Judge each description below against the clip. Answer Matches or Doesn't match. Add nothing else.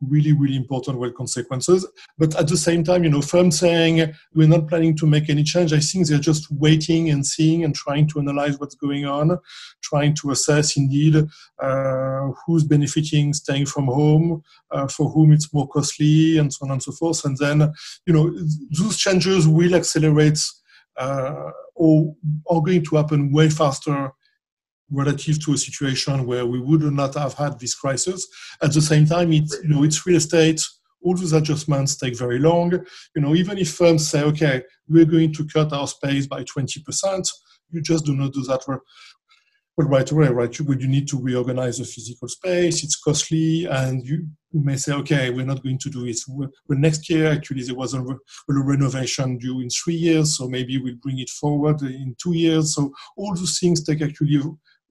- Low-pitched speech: Doesn't match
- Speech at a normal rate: Matches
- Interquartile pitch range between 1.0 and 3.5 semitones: Matches